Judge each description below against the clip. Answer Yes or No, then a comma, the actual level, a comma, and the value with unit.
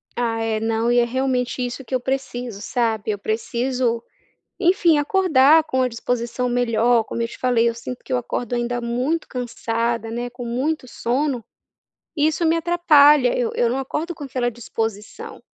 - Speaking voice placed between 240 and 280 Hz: Yes, high, 245 Hz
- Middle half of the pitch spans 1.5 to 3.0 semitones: Yes, narrow, 2.4 semitones